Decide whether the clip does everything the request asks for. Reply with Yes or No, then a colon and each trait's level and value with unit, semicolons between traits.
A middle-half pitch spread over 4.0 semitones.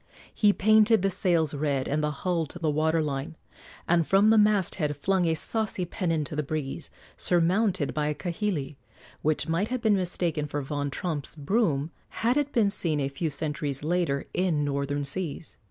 Yes: average, 4.4 semitones